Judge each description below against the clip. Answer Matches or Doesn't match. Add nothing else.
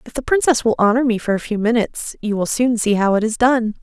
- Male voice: Doesn't match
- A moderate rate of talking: Doesn't match